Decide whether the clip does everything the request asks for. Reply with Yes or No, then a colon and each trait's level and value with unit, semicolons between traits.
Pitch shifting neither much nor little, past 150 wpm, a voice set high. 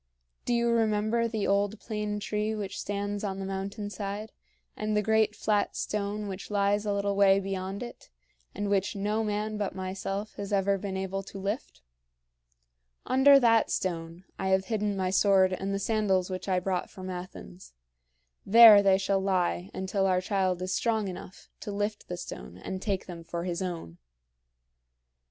No: narrow, 1.9 semitones; average, 175 wpm; high, 200 Hz